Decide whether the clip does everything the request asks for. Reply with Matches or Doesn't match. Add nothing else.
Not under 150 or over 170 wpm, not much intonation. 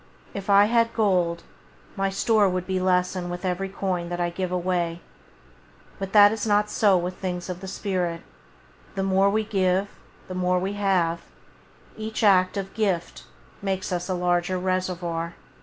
Matches